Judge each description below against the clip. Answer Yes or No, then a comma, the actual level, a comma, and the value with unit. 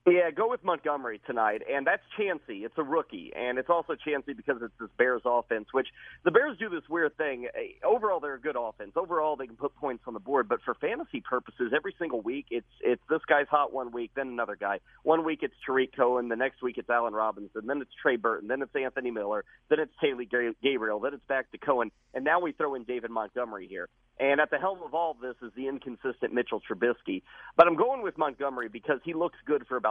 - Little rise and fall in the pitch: No, average, 4.4 semitones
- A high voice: No, low, 135 Hz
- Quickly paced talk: Yes, fast, 235 wpm